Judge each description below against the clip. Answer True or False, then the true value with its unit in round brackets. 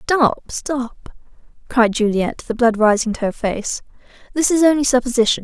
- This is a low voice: False (245 Hz)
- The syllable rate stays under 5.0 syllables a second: True (4.6 syllables/s)